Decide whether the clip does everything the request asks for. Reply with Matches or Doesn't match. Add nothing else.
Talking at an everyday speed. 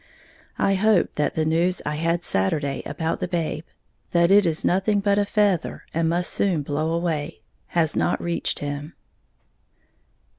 Matches